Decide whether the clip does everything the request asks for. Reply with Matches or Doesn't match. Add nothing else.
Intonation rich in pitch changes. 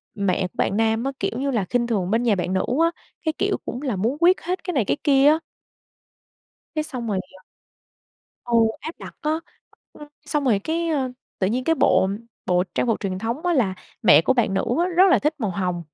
Matches